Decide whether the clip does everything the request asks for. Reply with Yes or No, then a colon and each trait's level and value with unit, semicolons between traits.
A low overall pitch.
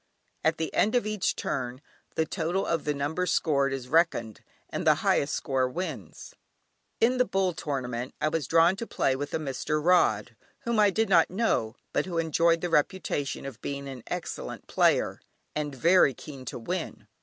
No: medium, 155 Hz